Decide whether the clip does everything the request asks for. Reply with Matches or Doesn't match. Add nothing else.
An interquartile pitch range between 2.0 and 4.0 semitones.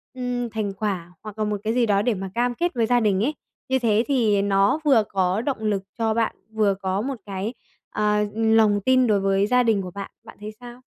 Matches